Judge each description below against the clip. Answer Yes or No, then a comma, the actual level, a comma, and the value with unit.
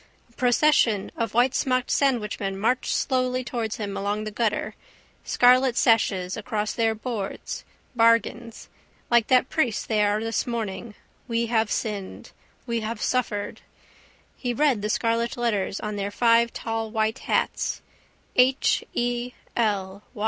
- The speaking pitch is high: Yes, high, 230 Hz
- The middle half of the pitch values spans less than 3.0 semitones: Yes, narrow, 2.4 semitones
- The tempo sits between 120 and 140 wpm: Yes, slow, 135 wpm